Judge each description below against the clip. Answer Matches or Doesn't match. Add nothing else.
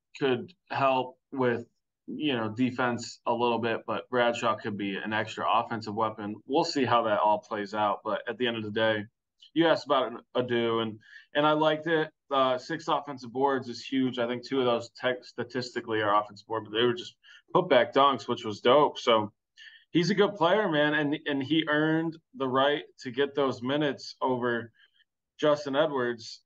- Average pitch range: Matches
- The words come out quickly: Doesn't match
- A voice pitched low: Matches